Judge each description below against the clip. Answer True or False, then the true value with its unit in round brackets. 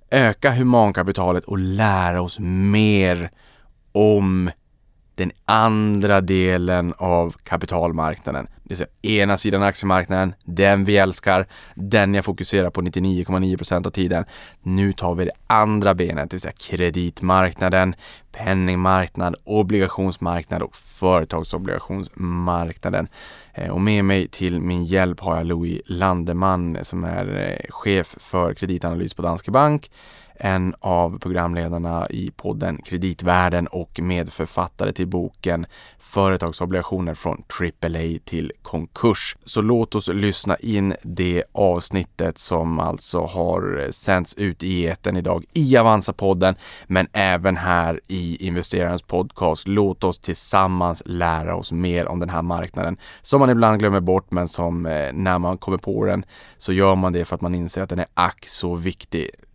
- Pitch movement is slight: True (2.0 semitones)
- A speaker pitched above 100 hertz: False (90 Hz)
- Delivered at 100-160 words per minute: True (135 wpm)